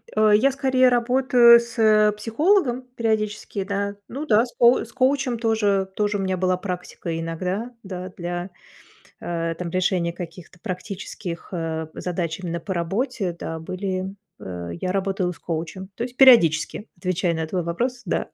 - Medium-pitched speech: No, high, 195 Hz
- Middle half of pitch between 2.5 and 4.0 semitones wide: No, average, 5.0 semitones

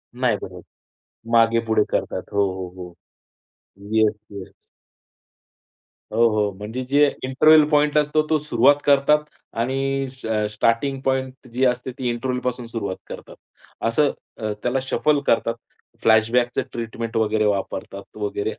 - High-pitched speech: No, low, 120 Hz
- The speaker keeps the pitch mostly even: No, average, 3.7 semitones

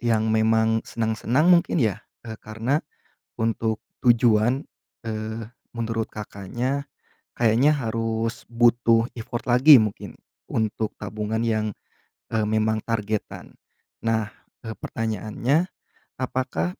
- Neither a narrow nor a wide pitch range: No, narrow, 1.6 semitones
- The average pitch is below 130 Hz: Yes, low, 115 Hz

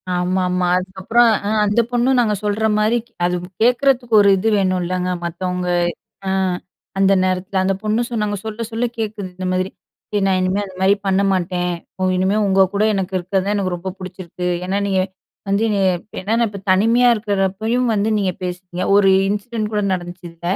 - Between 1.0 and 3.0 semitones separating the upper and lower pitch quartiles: Yes, narrow, 2.5 semitones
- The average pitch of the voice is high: Yes, high, 195 Hz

